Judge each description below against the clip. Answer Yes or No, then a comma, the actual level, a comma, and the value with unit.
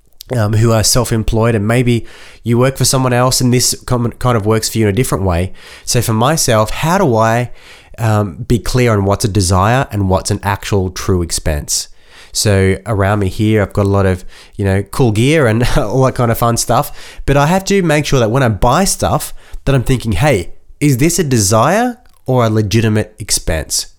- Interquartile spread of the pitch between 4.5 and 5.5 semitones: No, average, 3.8 semitones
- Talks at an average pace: No, fast, 210 wpm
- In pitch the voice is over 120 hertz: No, low, 115 Hz